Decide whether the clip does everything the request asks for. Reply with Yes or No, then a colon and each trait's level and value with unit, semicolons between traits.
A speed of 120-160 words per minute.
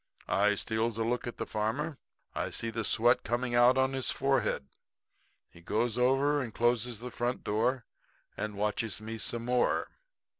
No: average, 175 wpm